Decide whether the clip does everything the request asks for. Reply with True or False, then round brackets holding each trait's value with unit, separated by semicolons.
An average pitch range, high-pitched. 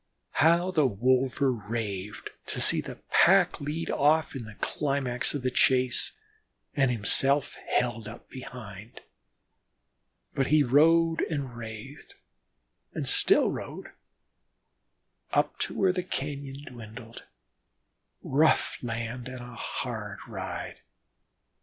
False (3.9 semitones; 130 Hz)